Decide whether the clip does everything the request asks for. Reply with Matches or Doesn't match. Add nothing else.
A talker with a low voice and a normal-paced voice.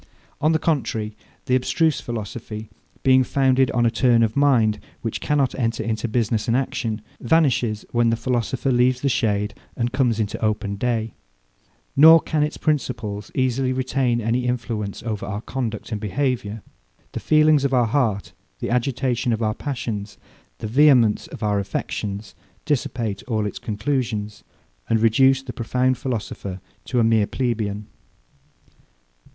Matches